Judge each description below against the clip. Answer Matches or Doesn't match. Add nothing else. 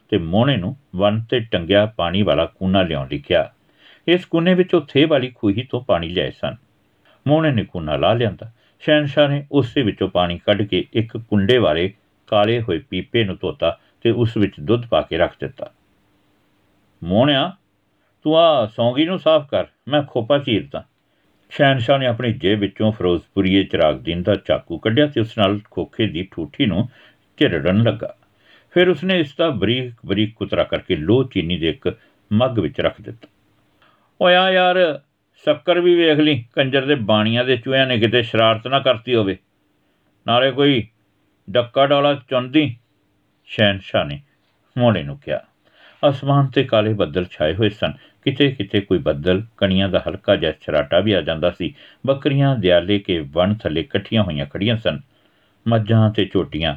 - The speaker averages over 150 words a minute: Matches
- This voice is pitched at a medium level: Doesn't match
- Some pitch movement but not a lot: Doesn't match